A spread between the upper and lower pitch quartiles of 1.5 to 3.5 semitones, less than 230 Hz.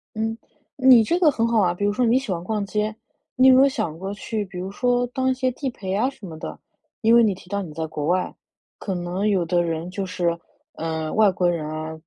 No: average, 5.2 semitones; high, 200 Hz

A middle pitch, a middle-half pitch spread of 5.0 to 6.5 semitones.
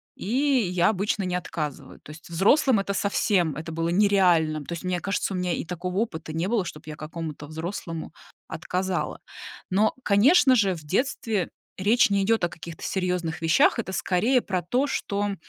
No: medium, 180 Hz; average, 3.7 semitones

